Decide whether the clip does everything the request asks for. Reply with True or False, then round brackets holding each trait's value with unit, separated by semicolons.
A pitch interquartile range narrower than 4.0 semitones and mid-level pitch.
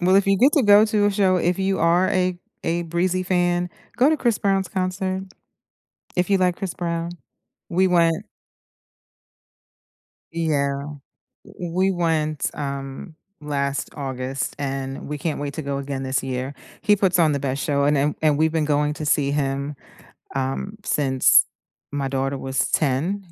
False (4.9 semitones; 160 Hz)